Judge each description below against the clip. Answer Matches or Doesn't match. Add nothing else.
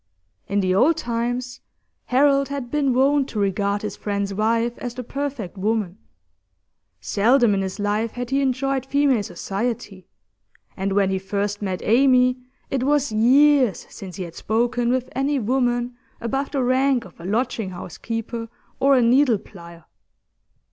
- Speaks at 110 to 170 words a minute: Matches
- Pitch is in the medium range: Doesn't match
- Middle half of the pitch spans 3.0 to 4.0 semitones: Doesn't match